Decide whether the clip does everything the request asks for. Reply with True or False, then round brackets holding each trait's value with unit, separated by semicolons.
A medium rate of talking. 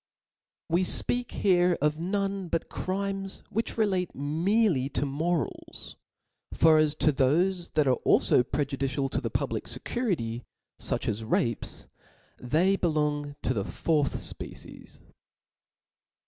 False (125 wpm)